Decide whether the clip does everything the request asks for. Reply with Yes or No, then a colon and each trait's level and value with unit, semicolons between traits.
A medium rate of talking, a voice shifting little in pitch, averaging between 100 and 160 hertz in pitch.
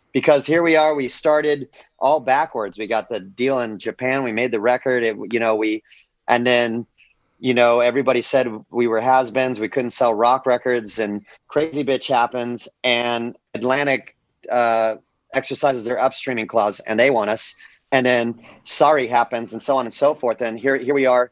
Yes: average, 185 wpm; narrow, 2.1 semitones; low, 125 Hz